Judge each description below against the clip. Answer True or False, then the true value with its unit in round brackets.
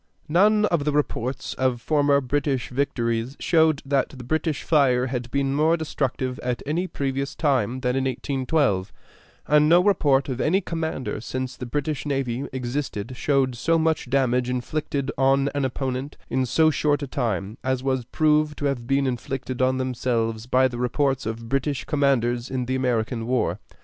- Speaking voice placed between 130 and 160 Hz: True (135 Hz)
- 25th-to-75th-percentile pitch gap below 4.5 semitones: True (2.6 semitones)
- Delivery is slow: False (170 wpm)